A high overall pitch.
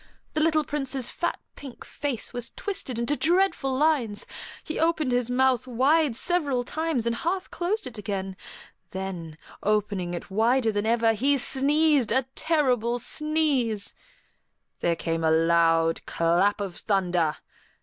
Yes: high, 245 Hz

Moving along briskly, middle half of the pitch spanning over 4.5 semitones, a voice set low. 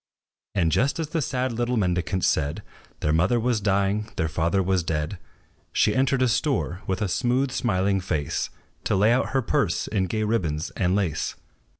No: average, 180 wpm; wide, 5.4 semitones; low, 100 Hz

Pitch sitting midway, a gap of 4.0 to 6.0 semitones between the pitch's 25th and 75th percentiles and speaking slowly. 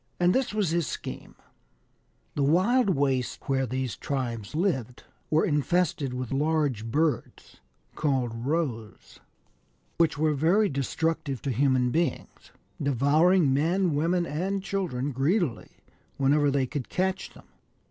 Yes: medium, 145 Hz; average, 4.6 semitones; slow, 125 wpm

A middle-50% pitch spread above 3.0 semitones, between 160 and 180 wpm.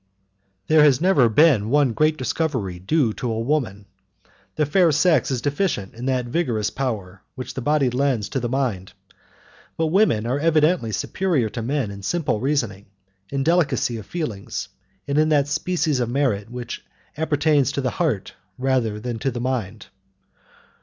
Yes: average, 5.0 semitones; average, 165 wpm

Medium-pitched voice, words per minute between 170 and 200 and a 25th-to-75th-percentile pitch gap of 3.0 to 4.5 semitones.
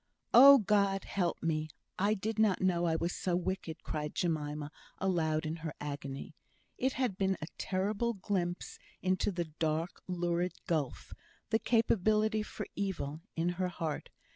No: medium, 180 Hz; average, 150 wpm; average, 3.8 semitones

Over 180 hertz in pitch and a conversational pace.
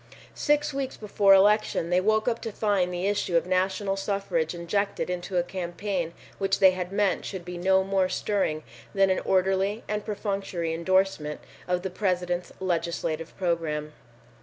Yes: high, 190 Hz; average, 160 wpm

